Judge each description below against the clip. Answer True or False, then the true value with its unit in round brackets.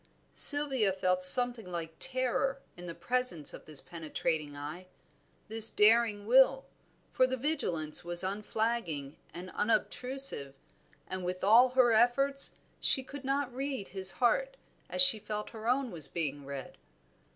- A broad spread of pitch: True (6.7 semitones)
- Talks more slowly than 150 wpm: True (140 wpm)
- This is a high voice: True (220 Hz)